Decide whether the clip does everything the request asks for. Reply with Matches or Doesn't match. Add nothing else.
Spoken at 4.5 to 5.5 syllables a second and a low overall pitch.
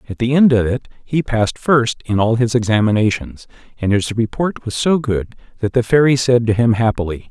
Matches